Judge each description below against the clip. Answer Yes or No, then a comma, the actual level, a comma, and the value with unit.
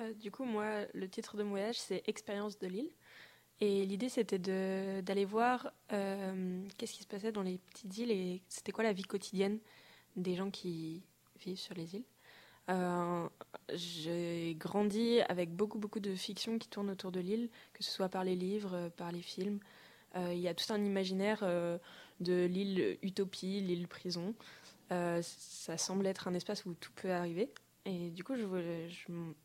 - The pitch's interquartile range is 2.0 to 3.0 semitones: Yes, average, 2.7 semitones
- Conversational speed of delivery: Yes, average, 185 wpm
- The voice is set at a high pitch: Yes, high, 195 Hz